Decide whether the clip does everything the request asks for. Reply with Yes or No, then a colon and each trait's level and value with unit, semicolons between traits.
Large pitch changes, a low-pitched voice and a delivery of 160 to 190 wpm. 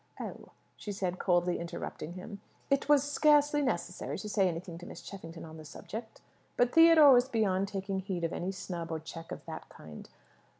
No: wide, 6.0 semitones; high, 190 Hz; average, 185 wpm